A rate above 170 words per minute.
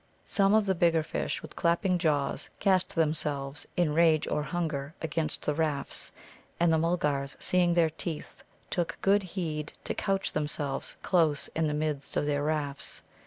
No: average, 165 wpm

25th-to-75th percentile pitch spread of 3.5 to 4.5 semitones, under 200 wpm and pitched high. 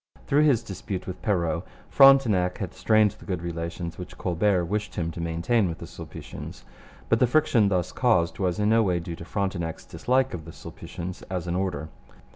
No: average, 4.2 semitones; average, 190 wpm; very low, 95 Hz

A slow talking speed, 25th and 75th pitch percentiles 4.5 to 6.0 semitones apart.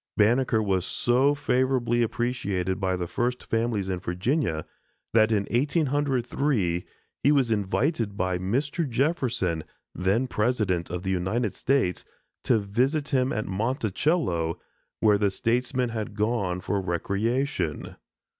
Yes: slow, 125 wpm; average, 5.3 semitones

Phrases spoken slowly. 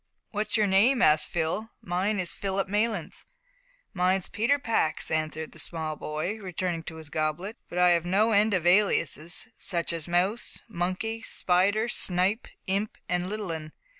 No: average, 155 wpm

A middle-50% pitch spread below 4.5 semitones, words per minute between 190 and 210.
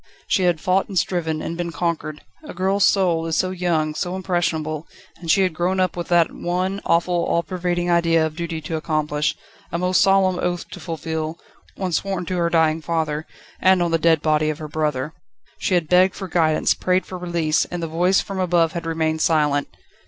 Yes: narrow, 2.4 semitones; fast, 205 wpm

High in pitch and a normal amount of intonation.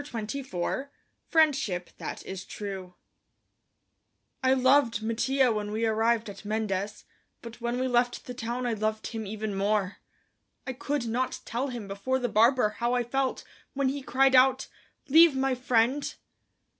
Yes: high, 240 Hz; average, 3.4 semitones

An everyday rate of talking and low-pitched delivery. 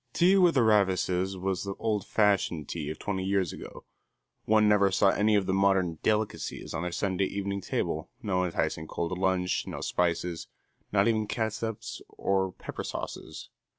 Yes: average, 165 wpm; very low, 95 Hz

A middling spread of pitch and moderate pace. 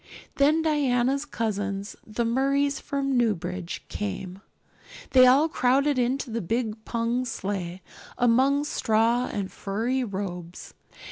No: average, 5.0 semitones; slow, 115 wpm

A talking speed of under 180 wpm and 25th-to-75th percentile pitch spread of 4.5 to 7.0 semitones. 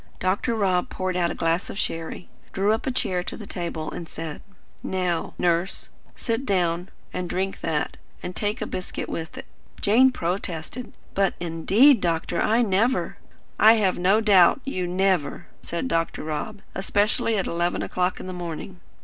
No: average, 170 wpm; average, 3.3 semitones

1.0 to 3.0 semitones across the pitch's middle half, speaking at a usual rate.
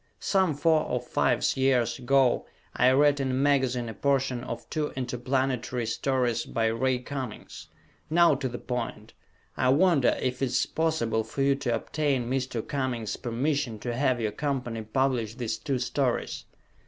Yes: narrow, 2.6 semitones; average, 160 wpm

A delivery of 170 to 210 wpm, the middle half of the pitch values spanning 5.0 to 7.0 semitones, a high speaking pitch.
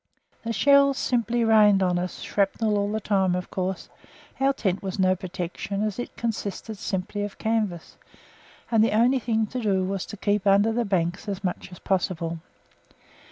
No: average, 175 wpm; average, 3.0 semitones; high, 205 Hz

